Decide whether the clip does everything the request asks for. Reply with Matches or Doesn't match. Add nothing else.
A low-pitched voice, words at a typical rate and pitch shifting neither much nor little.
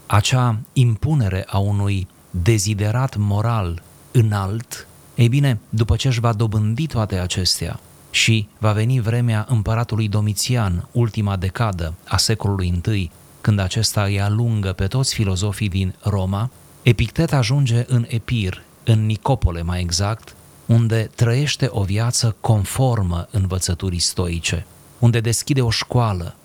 Matches